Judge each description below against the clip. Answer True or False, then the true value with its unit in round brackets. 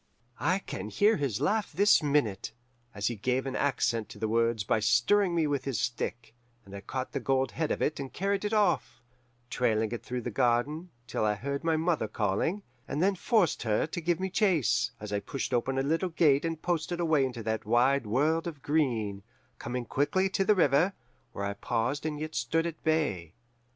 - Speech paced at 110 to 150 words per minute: False (200 wpm)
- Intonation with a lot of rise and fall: True (6.1 semitones)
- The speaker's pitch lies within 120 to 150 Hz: True (140 Hz)